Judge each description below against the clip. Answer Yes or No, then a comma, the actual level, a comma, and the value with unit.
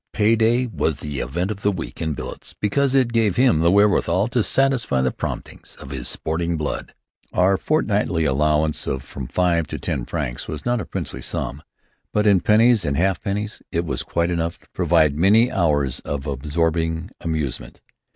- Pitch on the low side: Yes, very low, 85 Hz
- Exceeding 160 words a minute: Yes, average, 180 wpm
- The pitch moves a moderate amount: No, wide, 5.7 semitones